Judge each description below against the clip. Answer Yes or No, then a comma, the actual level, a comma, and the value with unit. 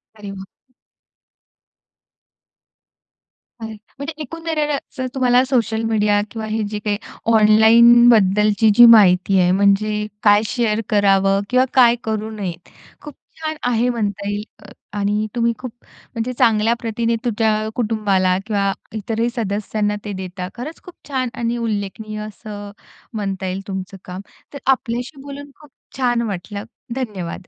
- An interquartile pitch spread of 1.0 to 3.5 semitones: Yes, average, 2.9 semitones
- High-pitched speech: Yes, high, 215 Hz